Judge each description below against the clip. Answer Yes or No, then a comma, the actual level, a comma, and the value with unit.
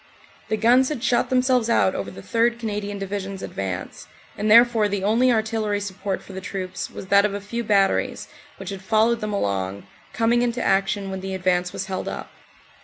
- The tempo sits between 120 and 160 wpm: No, average, 200 wpm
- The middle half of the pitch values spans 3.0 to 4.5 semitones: Yes, average, 3.3 semitones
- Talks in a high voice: Yes, high, 205 Hz